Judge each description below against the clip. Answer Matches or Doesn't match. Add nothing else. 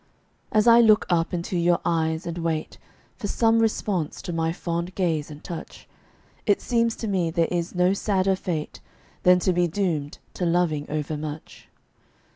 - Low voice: Doesn't match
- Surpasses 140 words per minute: Matches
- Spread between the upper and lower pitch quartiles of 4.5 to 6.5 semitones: Doesn't match